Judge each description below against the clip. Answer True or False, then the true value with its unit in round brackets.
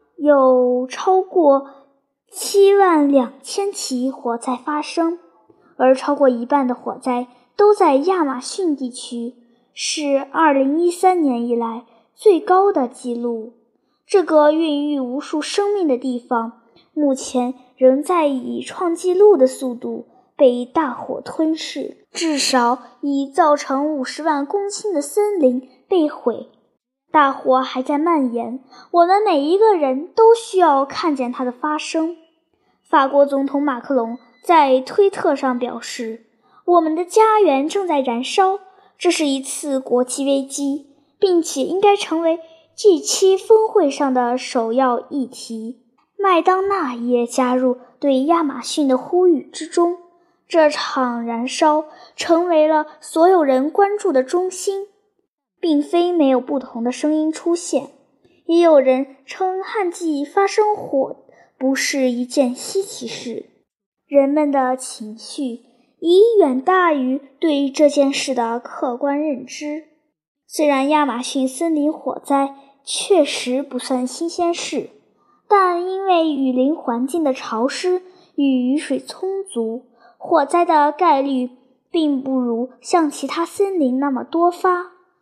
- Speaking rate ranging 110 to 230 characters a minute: True (190 characters per minute)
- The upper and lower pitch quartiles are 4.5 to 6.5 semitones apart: True (5.2 semitones)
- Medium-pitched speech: False (290 Hz)